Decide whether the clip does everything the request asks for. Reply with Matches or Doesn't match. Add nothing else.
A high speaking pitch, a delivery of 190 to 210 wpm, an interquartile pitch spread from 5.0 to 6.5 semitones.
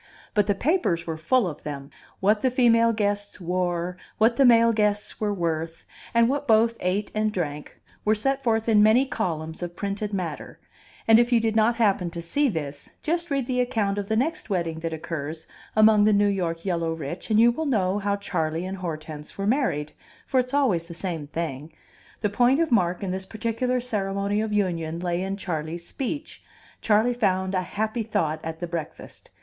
Matches